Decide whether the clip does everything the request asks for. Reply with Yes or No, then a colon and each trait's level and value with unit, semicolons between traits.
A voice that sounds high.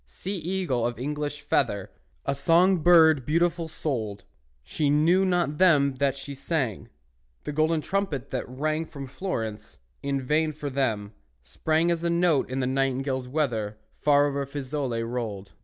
No: medium, 140 Hz